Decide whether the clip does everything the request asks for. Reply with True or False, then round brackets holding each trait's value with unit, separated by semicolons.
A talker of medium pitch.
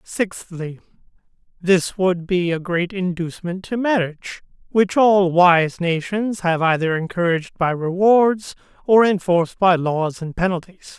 True (180 Hz)